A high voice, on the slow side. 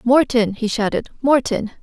Yes: high, 240 Hz; slow, 130 wpm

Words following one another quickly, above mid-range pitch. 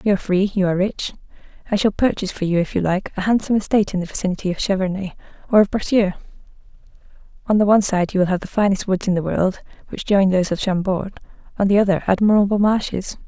Yes: fast, 215 wpm; high, 195 Hz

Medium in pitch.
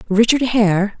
No: high, 215 Hz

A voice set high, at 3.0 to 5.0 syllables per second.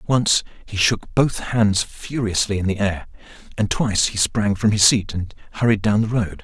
No: low, 105 Hz; 4.7 syllables/s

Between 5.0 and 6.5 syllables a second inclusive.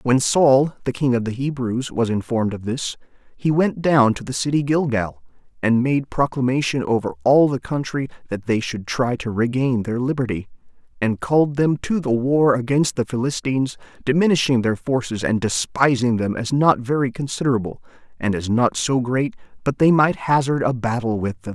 Yes: 5.1 syllables/s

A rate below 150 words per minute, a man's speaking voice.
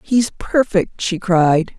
No: slow, 135 wpm; female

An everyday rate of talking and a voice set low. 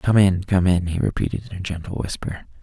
No: fast, 230 wpm; very low, 90 Hz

